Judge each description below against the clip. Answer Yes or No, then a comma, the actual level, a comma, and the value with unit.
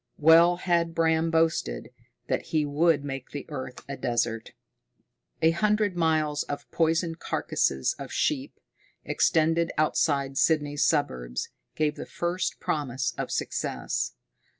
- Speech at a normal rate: No, slow, 125 wpm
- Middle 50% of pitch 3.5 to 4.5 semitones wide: No, average, 3.1 semitones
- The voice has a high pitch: No, medium, 155 Hz